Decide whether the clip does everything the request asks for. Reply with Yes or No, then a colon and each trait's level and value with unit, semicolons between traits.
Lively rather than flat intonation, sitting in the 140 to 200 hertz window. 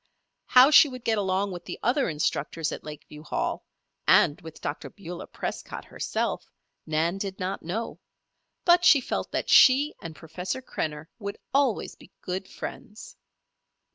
Yes: wide, 7.7 semitones; high, 190 Hz